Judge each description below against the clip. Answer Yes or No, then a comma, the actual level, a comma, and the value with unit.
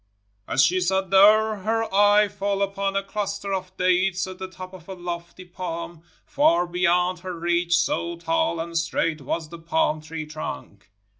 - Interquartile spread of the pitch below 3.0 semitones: Yes, narrow, 2.5 semitones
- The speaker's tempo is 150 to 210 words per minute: Yes, average, 170 wpm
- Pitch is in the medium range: Yes, medium, 180 Hz